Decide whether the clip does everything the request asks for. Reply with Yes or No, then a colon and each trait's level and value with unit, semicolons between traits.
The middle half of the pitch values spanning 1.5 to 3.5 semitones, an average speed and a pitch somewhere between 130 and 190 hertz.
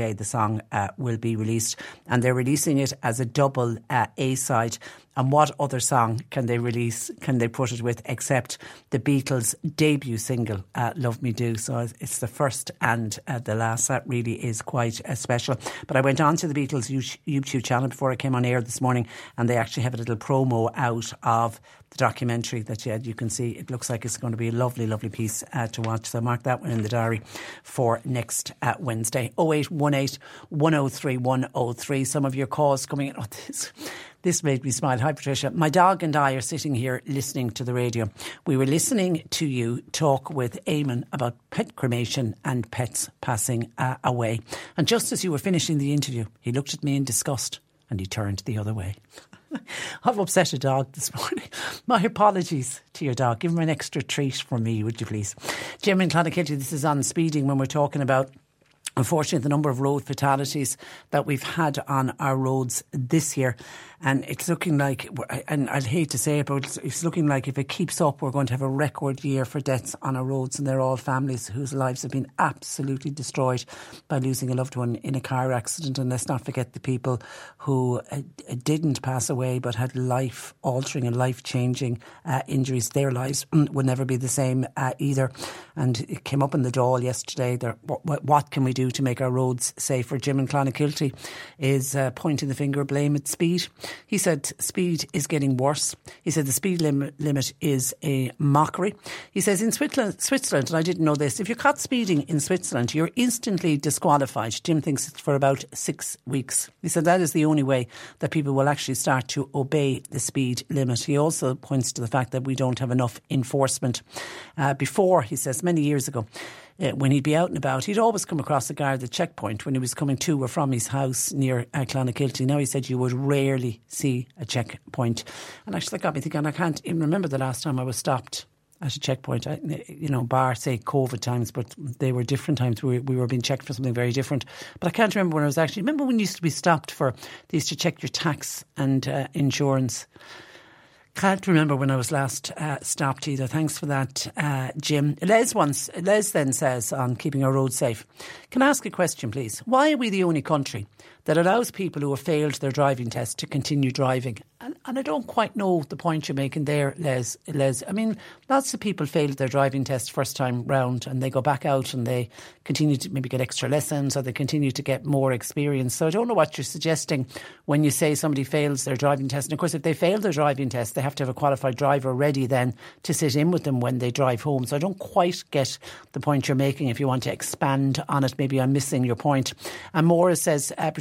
No: average, 3.0 semitones; fast, 220 wpm; low, 135 Hz